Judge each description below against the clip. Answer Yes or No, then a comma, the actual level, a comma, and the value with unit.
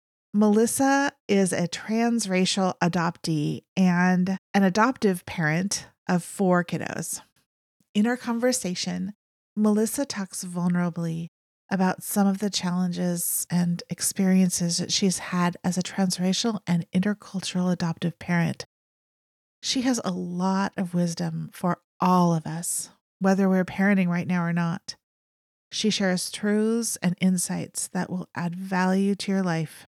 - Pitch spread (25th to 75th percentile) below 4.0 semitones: Yes, narrow, 2.4 semitones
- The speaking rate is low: Yes, slow, 130 wpm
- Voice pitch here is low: No, medium, 185 Hz